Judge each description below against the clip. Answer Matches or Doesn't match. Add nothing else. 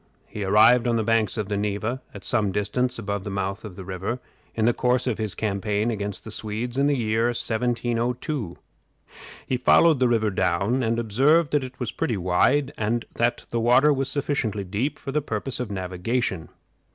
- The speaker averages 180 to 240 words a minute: Matches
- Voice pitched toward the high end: Doesn't match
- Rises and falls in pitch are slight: Doesn't match